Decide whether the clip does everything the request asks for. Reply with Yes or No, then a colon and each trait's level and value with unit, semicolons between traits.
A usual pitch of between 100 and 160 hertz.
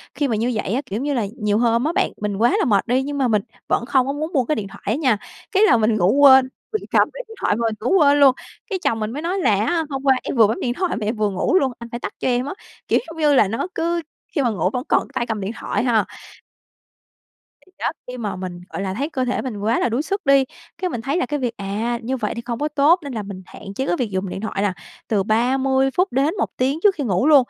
No: very high, 250 Hz